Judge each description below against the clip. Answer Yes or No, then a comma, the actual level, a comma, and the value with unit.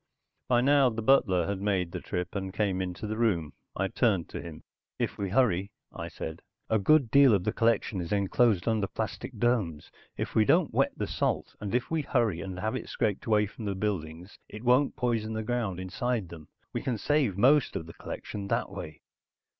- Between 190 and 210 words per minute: Yes, fast, 205 wpm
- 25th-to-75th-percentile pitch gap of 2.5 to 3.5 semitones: No, average, 4.4 semitones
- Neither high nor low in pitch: No, low, 105 Hz